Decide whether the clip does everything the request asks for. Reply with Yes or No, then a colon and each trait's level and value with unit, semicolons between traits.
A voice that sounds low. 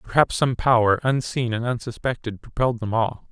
Yes: low, 120 Hz